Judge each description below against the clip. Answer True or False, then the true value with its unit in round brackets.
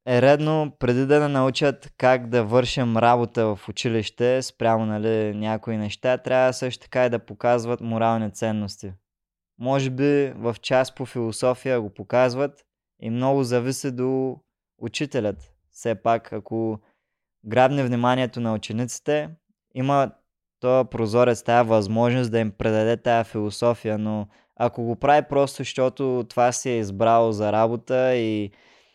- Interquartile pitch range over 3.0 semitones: False (2.5 semitones)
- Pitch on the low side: True (120 Hz)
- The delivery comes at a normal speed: True (140 wpm)